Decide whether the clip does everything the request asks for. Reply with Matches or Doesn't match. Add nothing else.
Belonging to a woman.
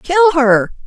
Matches